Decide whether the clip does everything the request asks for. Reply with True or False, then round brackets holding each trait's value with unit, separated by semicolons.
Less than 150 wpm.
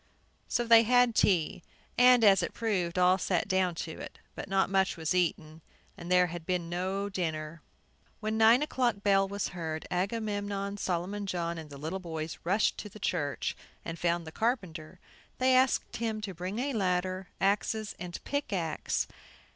False (170 wpm)